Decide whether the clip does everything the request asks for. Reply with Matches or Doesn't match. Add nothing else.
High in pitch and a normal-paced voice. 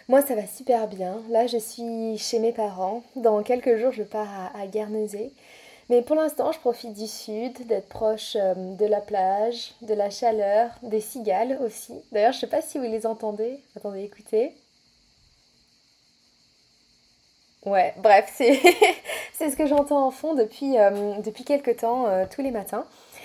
Matches